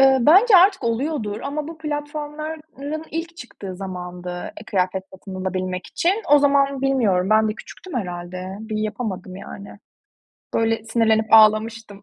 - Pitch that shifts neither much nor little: No, wide, 7.3 semitones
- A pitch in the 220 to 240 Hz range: Yes, high, 225 Hz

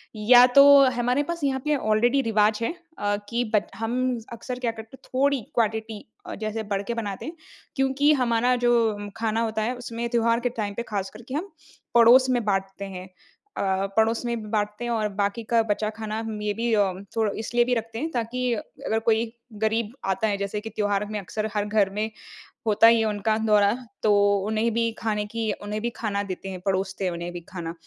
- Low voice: No, high, 220 Hz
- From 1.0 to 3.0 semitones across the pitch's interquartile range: Yes, narrow, 2.4 semitones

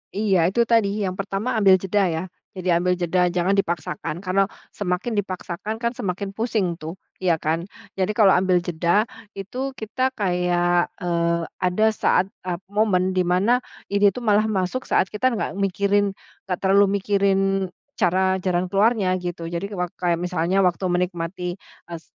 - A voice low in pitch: No, medium, 185 Hz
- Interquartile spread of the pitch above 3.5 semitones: No, narrow, 2.4 semitones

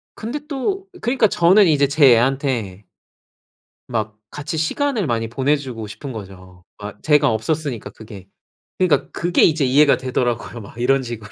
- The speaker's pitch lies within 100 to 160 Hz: Yes, low, 135 Hz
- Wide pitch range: Yes, wide, 5.8 semitones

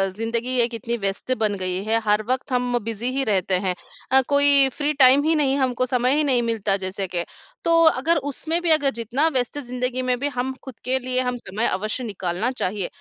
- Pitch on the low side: No, very high, 250 Hz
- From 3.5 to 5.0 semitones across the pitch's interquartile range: Yes, average, 3.9 semitones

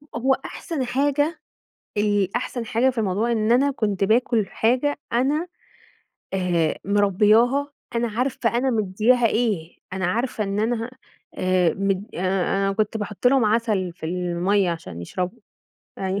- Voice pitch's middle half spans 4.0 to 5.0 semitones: Yes, average, 4.3 semitones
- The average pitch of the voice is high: Yes, high, 215 Hz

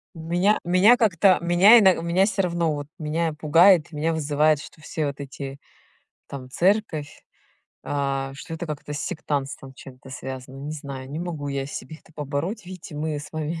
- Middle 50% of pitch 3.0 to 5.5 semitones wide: Yes, average, 3.5 semitones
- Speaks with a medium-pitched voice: Yes, medium, 155 Hz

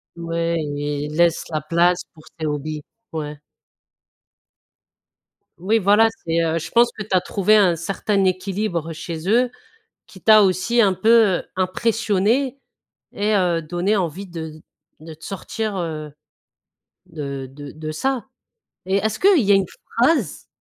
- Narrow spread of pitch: No, average, 4.7 semitones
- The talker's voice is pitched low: No, medium, 180 Hz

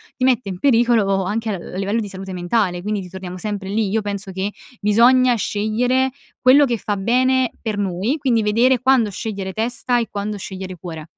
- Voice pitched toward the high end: Yes, high, 210 Hz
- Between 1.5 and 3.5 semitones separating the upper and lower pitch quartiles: No, average, 3.9 semitones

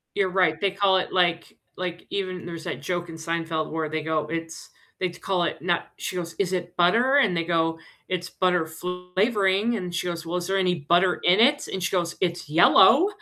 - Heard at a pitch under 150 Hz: No, medium, 180 Hz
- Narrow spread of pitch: Yes, narrow, 2.1 semitones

